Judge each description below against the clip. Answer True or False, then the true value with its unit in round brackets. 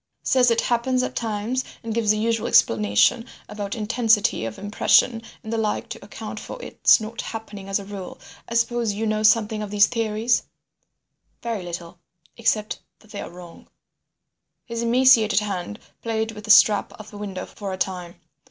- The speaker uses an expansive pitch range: False (2.4 semitones)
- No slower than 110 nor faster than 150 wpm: False (170 wpm)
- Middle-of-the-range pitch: False (215 Hz)